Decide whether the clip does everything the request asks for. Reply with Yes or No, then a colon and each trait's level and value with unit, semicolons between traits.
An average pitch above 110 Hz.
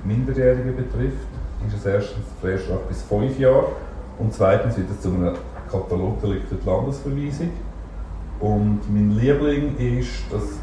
No: low, 105 Hz